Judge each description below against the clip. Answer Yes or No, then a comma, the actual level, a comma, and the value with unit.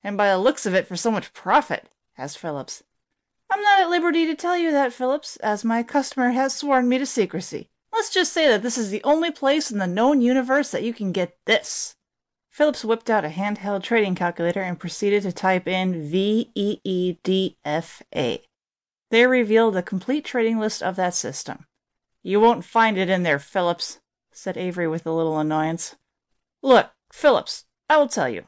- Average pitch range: No, wide, 6.1 semitones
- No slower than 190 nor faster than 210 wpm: Yes, average, 195 wpm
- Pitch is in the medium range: No, high, 215 Hz